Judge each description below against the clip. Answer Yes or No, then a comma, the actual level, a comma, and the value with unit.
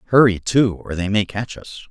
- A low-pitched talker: Yes, low, 105 Hz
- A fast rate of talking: Yes, fast, 220 wpm